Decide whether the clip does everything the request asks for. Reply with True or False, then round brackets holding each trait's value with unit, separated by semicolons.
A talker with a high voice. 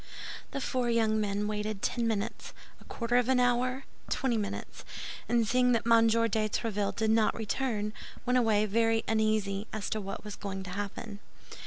True (220 Hz)